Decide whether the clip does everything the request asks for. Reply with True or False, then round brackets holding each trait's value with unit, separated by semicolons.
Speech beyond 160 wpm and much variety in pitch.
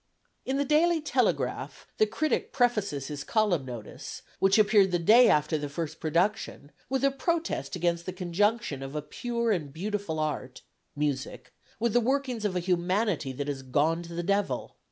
True (175 wpm; 7.1 semitones)